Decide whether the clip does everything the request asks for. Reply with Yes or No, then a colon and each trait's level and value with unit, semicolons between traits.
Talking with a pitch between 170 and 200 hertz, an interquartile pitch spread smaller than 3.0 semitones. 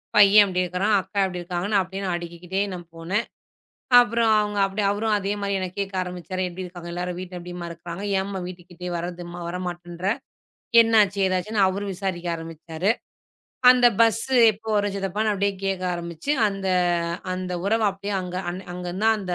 Yes: medium, 185 Hz; narrow, 2.4 semitones